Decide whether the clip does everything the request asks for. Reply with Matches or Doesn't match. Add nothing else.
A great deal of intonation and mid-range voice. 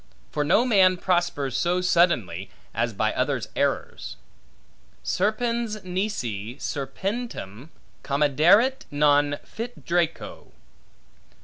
Matches